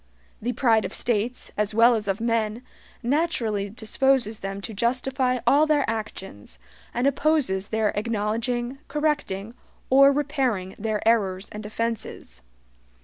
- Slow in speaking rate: Yes, slow, 130 wpm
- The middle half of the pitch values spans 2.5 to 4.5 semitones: Yes, average, 3.7 semitones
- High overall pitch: Yes, high, 230 Hz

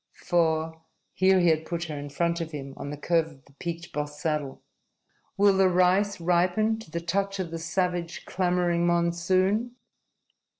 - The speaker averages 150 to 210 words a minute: Yes, average, 170 wpm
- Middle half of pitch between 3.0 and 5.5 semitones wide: No, narrow, 2.5 semitones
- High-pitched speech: No, medium, 170 Hz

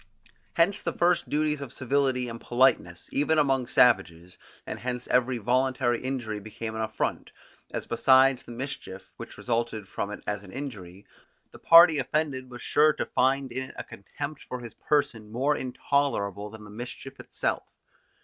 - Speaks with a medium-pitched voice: No, low, 125 Hz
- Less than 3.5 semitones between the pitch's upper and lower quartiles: No, average, 3.9 semitones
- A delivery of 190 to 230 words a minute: No, average, 165 wpm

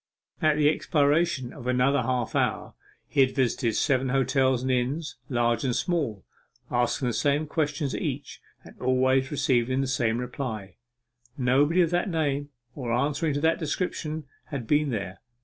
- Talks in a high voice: No, low, 135 Hz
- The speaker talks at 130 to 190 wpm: Yes, average, 160 wpm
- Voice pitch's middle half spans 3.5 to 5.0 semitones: No, average, 3.1 semitones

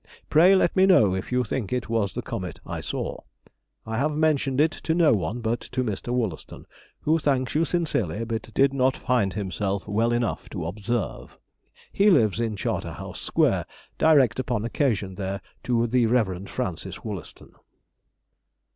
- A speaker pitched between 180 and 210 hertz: No, low, 120 Hz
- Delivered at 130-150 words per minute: No, average, 165 wpm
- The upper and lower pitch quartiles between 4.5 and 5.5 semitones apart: Yes, average, 4.8 semitones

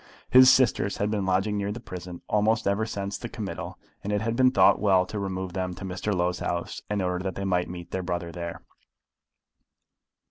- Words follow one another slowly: No, fast, 205 wpm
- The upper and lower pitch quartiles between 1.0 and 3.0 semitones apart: Yes, narrow, 2.6 semitones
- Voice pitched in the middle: No, very low, 95 Hz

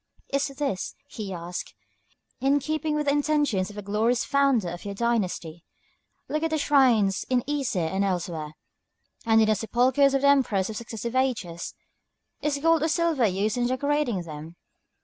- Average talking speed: Yes, average, 170 wpm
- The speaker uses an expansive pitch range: Yes, wide, 6.5 semitones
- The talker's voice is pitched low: No, high, 235 Hz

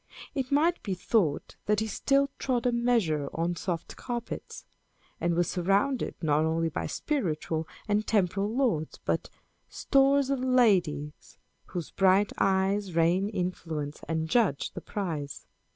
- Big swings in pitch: Yes, wide, 6.6 semitones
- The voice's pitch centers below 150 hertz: No, high, 190 Hz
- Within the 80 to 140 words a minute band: Yes, slow, 135 wpm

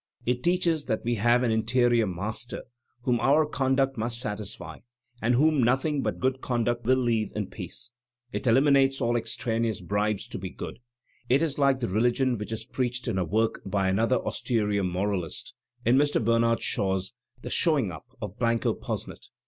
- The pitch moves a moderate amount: Yes, average, 3.3 semitones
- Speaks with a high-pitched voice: No, low, 120 Hz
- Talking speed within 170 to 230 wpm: Yes, average, 175 wpm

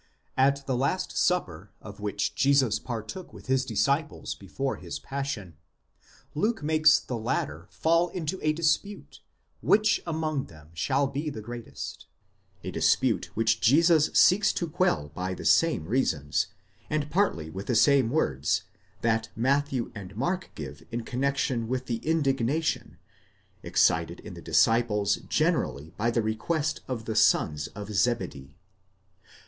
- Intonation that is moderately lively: No, wide, 6.2 semitones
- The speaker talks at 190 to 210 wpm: No, average, 145 wpm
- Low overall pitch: Yes, low, 130 Hz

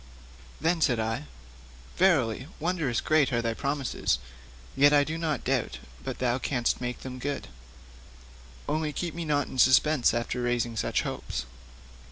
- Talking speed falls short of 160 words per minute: Yes, average, 150 wpm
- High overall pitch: No, low, 135 Hz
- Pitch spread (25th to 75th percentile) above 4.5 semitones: No, average, 4.1 semitones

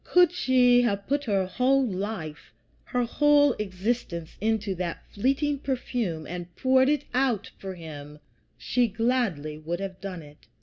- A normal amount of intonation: No, wide, 6.5 semitones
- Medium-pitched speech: No, high, 215 Hz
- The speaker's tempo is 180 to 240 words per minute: No, average, 145 wpm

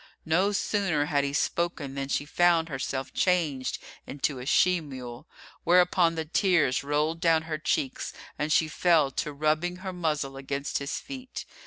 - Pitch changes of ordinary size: Yes, average, 3.8 semitones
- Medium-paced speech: Yes, average, 160 wpm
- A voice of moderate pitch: Yes, medium, 155 Hz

